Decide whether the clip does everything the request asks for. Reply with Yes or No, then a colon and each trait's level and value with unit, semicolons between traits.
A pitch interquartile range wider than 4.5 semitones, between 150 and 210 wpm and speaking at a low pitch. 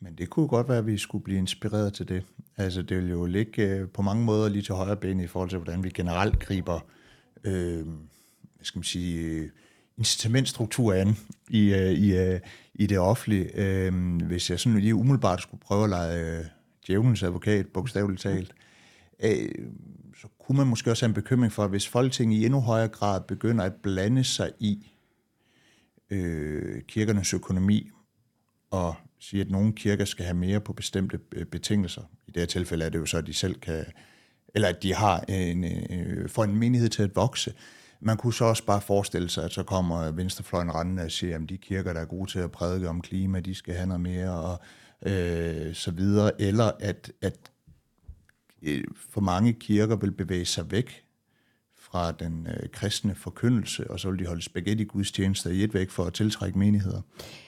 No: average, 3.1 semitones; average, 185 wpm; very low, 95 Hz